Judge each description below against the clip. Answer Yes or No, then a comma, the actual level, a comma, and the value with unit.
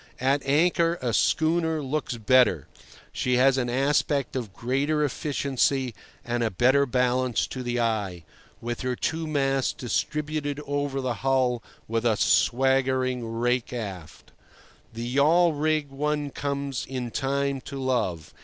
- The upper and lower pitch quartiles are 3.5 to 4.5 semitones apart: No, average, 2.8 semitones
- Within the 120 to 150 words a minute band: Yes, slow, 135 wpm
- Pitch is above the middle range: No, low, 130 Hz